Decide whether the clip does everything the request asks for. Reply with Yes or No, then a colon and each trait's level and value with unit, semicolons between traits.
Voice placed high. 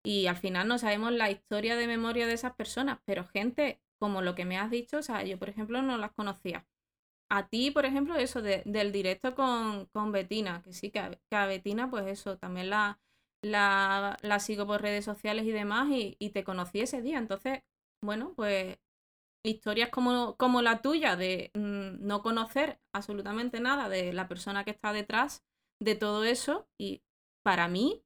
Yes: high, 210 Hz